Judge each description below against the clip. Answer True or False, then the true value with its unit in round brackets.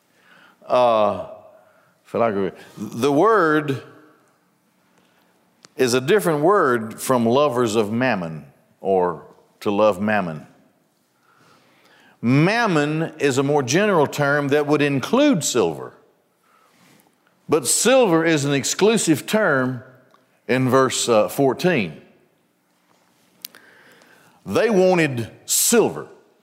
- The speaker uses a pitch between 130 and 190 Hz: True (135 Hz)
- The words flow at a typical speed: False (85 wpm)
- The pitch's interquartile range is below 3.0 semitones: False (5.6 semitones)